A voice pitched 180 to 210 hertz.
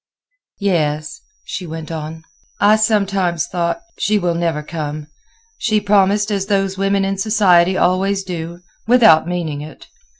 Yes: medium, 185 Hz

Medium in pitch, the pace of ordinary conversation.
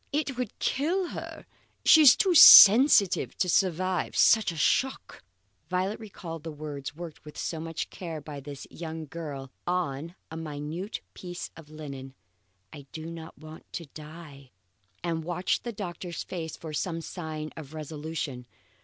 Yes: medium, 165 Hz; average, 150 wpm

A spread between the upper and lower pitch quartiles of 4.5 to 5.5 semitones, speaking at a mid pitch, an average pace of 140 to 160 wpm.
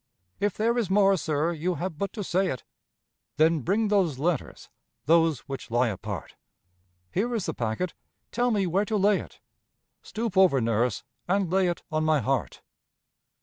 No: average, 5.1 semitones; medium, 175 Hz; average, 170 wpm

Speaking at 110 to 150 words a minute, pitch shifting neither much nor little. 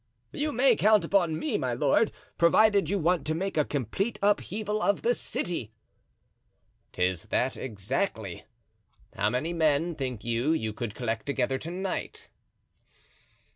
No: average, 140 wpm; wide, 8.5 semitones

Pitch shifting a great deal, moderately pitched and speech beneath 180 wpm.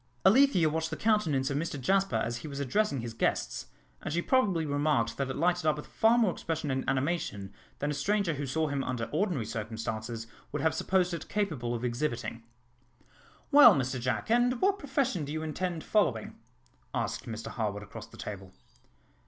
No: wide, 7.6 semitones; medium, 150 Hz; average, 185 wpm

